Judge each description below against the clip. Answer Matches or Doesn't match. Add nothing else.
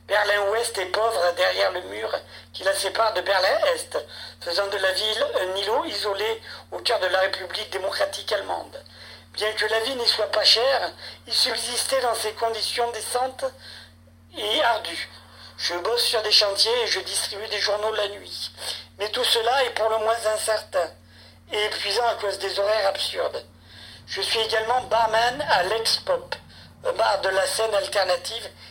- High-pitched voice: Matches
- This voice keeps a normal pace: Matches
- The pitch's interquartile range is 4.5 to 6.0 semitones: Doesn't match